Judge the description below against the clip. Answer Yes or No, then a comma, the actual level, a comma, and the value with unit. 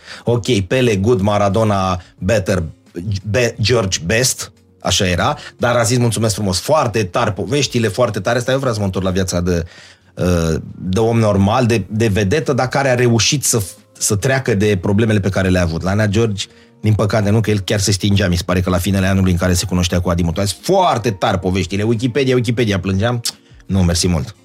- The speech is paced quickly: Yes, fast, 200 wpm